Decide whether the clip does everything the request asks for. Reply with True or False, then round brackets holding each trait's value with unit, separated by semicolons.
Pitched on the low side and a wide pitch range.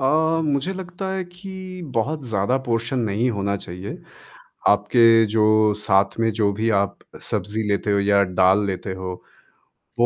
True (110 Hz; 6.6 semitones)